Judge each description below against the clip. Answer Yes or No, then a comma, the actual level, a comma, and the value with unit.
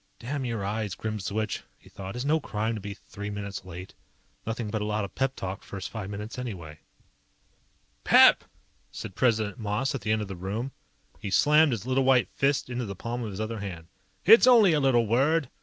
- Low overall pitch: Yes, low, 110 Hz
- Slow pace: No, fast, 205 wpm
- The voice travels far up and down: No, average, 4.2 semitones